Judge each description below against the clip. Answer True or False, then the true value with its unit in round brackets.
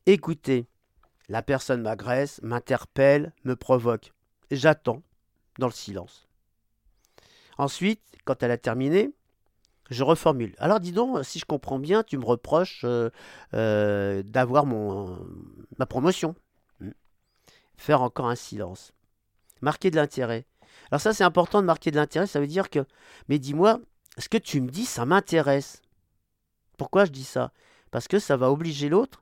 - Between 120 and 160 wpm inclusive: True (150 wpm)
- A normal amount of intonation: False (6.2 semitones)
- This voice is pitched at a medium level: False (130 Hz)